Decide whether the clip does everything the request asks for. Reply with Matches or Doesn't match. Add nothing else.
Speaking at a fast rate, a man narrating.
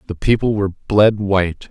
Doesn't match